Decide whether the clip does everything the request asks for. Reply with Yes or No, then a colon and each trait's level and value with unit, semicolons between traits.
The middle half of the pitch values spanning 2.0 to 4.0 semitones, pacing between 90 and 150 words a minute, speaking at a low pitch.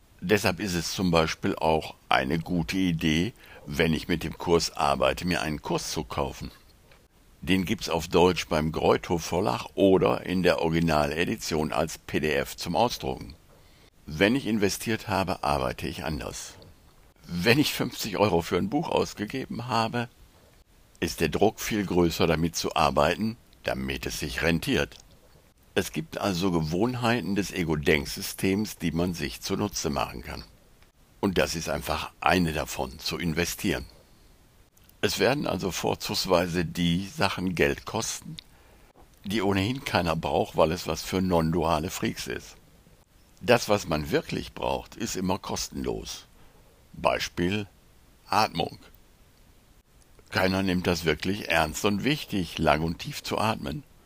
Yes: average, 3.6 semitones; average, 140 wpm; very low, 90 Hz